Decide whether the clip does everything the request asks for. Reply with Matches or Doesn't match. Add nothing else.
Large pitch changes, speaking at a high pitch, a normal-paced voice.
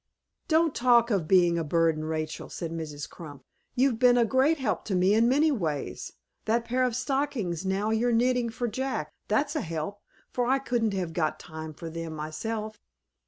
Matches